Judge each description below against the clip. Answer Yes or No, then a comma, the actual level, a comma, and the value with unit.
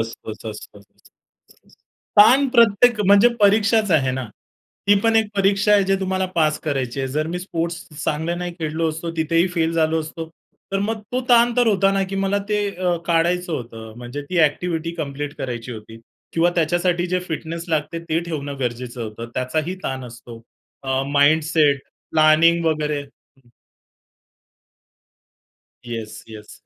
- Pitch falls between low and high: Yes, medium, 160 Hz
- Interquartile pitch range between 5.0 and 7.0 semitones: Yes, wide, 5.4 semitones